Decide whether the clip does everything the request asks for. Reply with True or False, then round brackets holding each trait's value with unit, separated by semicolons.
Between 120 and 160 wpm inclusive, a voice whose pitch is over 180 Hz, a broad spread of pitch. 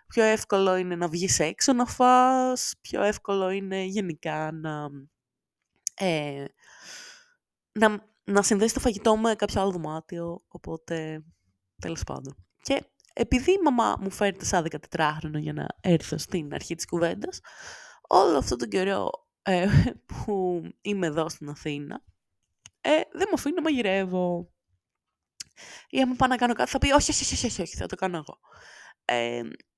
True (155 wpm; 190 Hz; 7.0 semitones)